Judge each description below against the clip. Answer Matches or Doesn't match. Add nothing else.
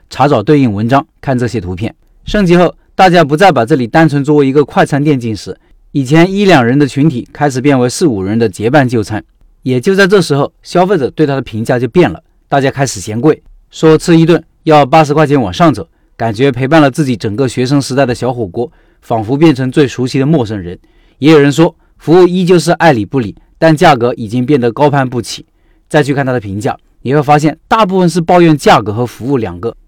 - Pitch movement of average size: Matches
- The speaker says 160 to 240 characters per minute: Doesn't match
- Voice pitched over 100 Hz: Matches